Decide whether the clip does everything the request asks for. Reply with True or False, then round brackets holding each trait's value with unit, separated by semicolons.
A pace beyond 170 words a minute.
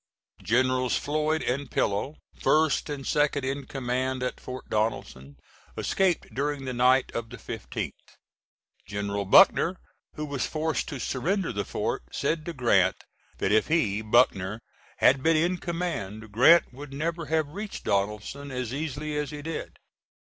False (150 wpm)